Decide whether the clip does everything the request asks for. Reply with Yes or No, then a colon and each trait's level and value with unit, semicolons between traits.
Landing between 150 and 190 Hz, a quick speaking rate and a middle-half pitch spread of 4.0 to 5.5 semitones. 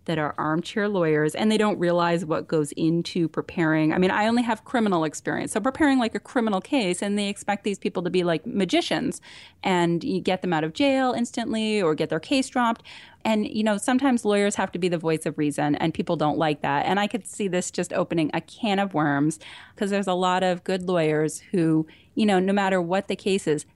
Yes: medium, 185 Hz; fast, 230 wpm; average, 4.5 semitones